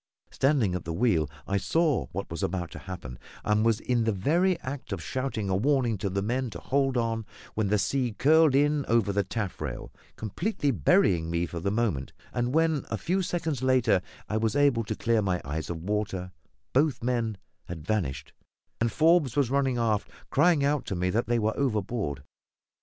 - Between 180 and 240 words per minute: Yes, average, 190 wpm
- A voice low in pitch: Yes, low, 115 Hz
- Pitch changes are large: Yes, wide, 6.0 semitones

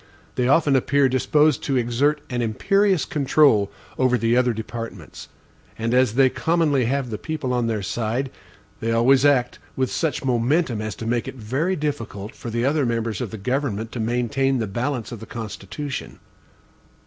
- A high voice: No, low, 125 Hz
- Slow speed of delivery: No, average, 170 wpm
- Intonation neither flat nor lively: Yes, average, 3.6 semitones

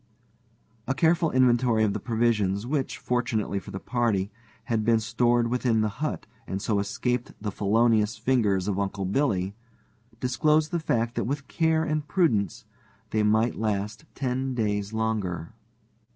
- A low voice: Yes, low, 115 Hz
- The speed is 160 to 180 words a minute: No, average, 150 wpm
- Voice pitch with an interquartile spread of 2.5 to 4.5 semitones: Yes, average, 3.9 semitones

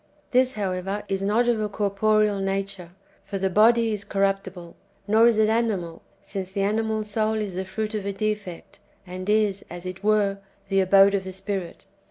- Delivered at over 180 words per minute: Yes, average, 190 wpm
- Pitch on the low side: No, high, 200 Hz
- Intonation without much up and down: Yes, narrow, 2.0 semitones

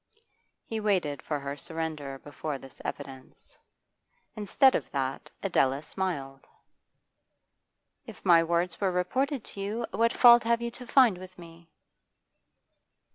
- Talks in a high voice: No, medium, 175 Hz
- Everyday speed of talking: No, slow, 130 wpm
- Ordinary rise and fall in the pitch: No, wide, 7.1 semitones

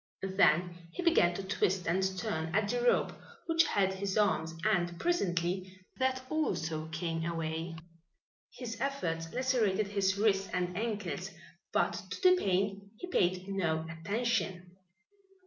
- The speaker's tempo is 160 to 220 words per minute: No, slow, 135 wpm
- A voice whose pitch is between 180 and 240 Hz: Yes, high, 190 Hz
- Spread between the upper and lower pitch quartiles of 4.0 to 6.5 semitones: Yes, average, 4.4 semitones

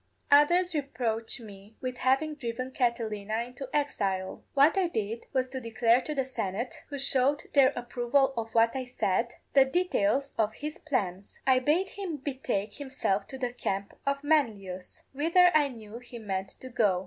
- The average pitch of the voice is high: Yes, very high, 255 Hz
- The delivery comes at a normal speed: Yes, average, 170 wpm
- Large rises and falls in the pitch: No, average, 4.3 semitones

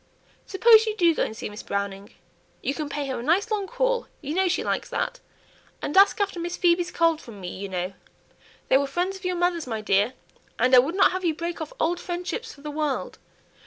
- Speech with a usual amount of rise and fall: No, wide, 6.3 semitones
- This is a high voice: Yes, very high, 335 Hz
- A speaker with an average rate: No, fast, 230 wpm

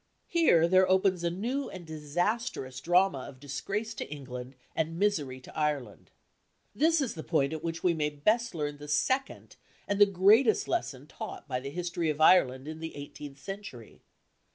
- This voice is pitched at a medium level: Yes, medium, 165 Hz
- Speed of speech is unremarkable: Yes, average, 175 wpm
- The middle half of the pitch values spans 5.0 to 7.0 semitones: Yes, wide, 5.6 semitones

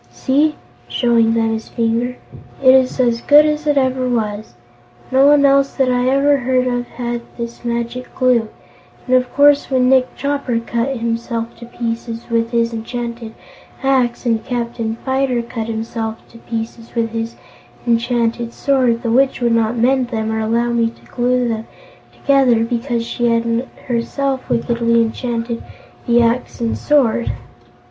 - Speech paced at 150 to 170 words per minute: Yes, average, 155 wpm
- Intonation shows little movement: Yes, narrow, 1.9 semitones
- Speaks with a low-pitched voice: No, high, 235 Hz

